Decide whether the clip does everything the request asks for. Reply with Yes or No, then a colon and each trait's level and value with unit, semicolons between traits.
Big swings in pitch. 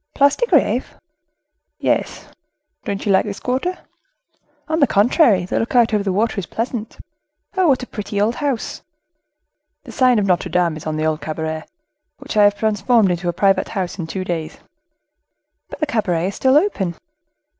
Yes: wide, 5.7 semitones